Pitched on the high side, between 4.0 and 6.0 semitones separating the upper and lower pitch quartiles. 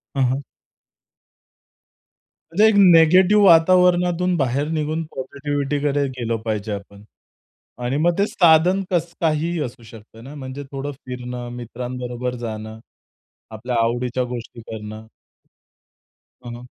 No: low, 135 Hz; wide, 5.5 semitones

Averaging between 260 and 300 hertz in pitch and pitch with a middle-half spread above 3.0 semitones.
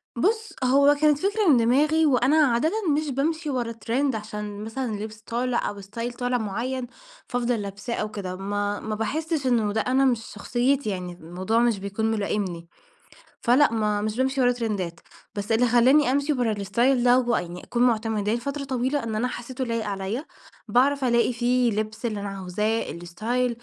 No: high, 235 Hz; average, 3.6 semitones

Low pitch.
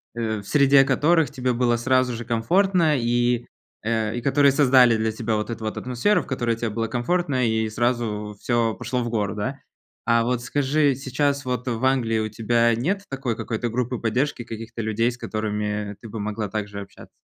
Yes: low, 120 Hz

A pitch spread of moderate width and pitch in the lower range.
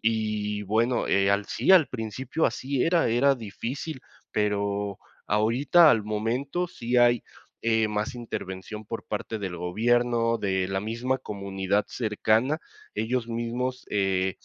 Yes: average, 3.2 semitones; low, 110 Hz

